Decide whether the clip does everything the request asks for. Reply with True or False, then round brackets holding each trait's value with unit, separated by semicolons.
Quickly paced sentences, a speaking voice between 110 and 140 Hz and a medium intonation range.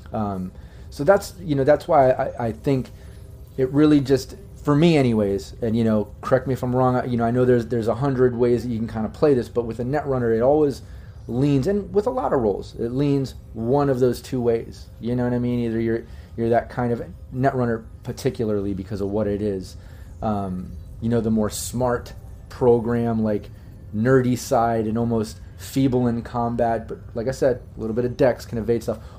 True (215 wpm; 115 Hz; 3.6 semitones)